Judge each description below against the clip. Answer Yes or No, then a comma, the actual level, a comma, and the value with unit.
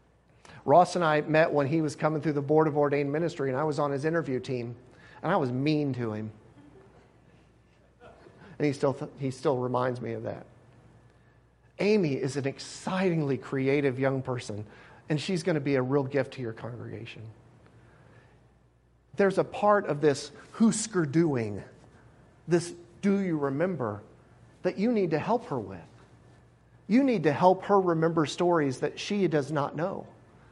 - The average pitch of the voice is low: No, medium, 145 Hz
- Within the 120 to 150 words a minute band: No, average, 165 wpm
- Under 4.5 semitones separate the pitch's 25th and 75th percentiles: No, average, 5.0 semitones